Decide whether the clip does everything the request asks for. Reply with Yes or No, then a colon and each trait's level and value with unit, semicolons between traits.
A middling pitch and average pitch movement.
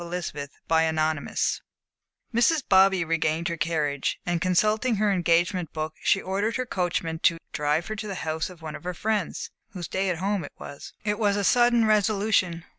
Yes: medium, 180 Hz; average, 4.2 semitones